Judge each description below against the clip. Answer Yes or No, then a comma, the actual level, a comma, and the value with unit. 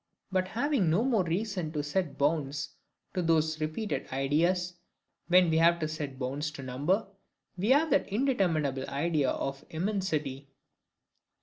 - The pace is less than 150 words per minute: Yes, average, 140 wpm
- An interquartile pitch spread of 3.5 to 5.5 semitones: Yes, average, 4.6 semitones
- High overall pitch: No, medium, 160 Hz